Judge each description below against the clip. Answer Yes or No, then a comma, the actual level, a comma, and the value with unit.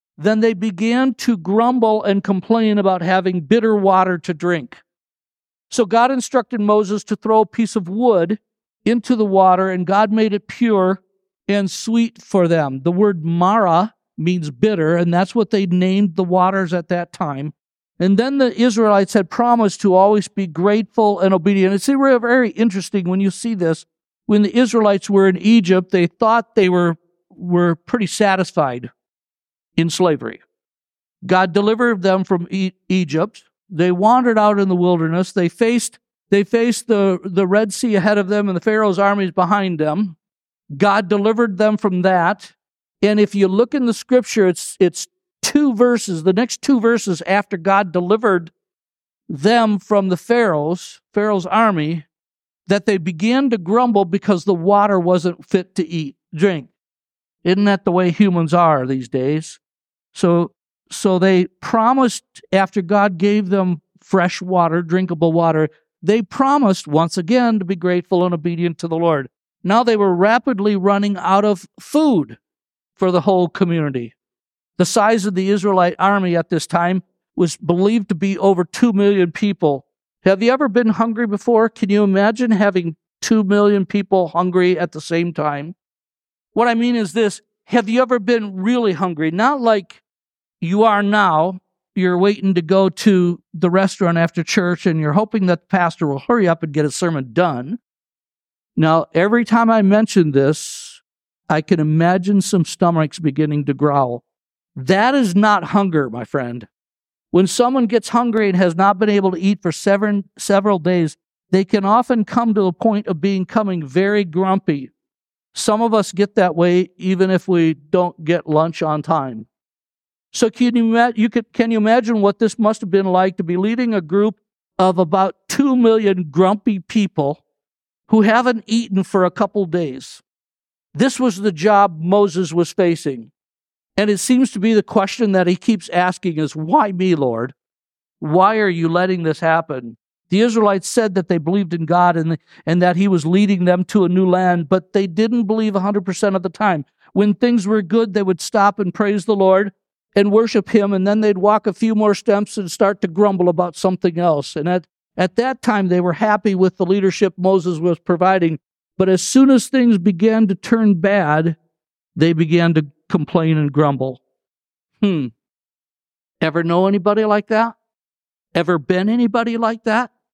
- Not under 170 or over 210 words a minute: Yes, average, 175 wpm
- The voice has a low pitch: No, high, 195 Hz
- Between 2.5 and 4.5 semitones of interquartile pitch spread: Yes, average, 3.4 semitones